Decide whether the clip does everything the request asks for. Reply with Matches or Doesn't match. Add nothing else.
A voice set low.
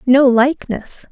Doesn't match